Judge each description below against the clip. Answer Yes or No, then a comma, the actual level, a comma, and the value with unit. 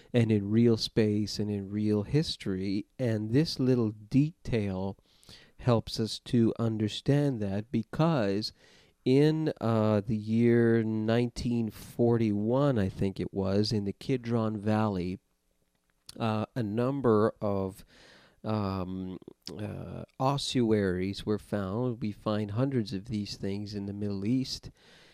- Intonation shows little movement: No, average, 3.0 semitones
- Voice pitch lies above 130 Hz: No, low, 110 Hz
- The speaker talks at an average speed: No, slow, 120 wpm